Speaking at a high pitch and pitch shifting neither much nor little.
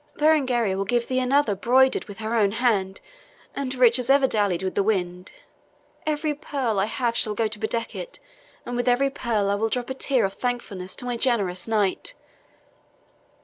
Yes: high, 235 Hz; average, 4.1 semitones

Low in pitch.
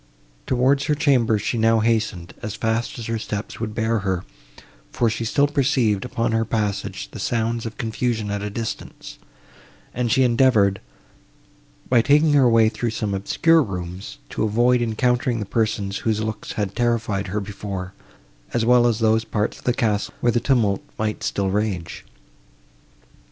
Yes: low, 110 Hz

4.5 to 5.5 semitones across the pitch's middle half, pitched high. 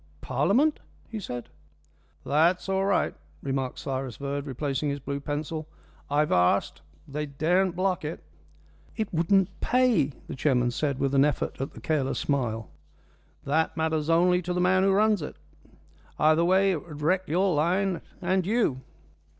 No: average, 5.0 semitones; medium, 160 Hz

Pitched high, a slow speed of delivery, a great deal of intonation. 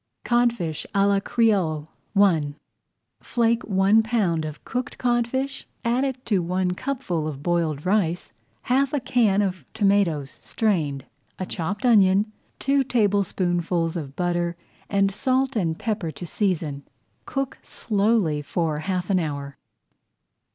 Yes: high, 195 Hz; slow, 130 wpm; wide, 5.8 semitones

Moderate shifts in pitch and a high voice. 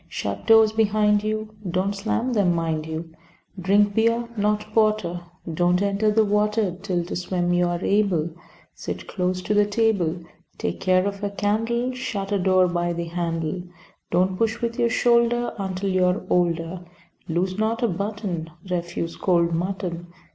Yes: average, 3.5 semitones; high, 195 Hz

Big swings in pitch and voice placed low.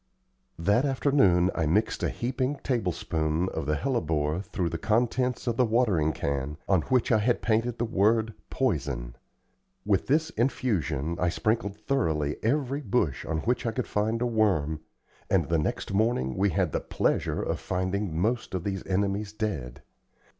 Yes: wide, 6.6 semitones; low, 100 Hz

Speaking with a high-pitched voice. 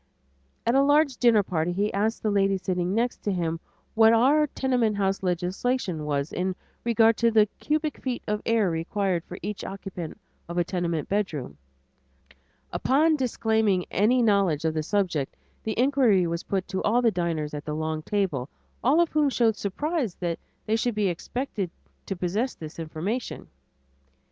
Yes: high, 200 Hz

